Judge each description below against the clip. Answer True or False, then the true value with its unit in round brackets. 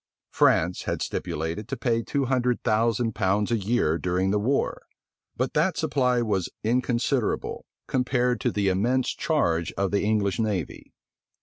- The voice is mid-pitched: False (110 Hz)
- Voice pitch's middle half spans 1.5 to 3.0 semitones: False (4.2 semitones)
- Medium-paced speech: True (145 wpm)